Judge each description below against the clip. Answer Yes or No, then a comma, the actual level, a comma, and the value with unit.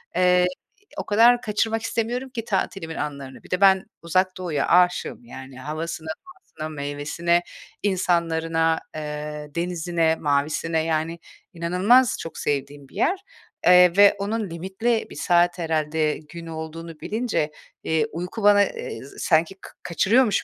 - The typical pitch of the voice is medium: Yes, medium, 170 Hz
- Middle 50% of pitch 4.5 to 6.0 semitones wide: No, average, 3.8 semitones